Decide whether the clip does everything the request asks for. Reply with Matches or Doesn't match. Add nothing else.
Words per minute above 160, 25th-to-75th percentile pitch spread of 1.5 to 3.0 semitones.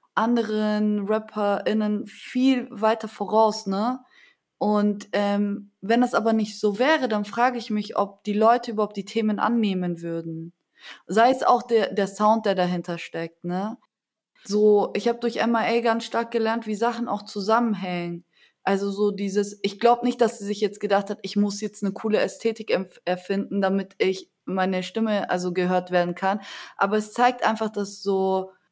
Matches